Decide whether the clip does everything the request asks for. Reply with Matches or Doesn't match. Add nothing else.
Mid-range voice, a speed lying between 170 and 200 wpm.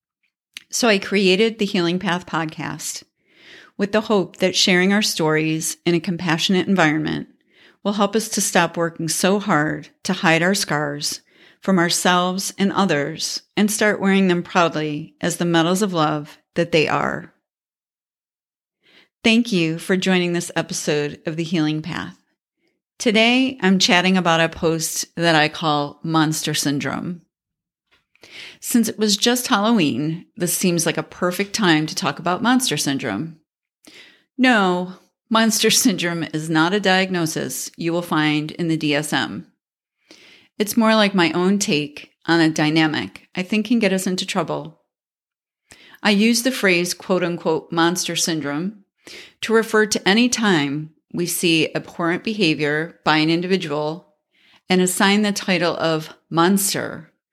Doesn't match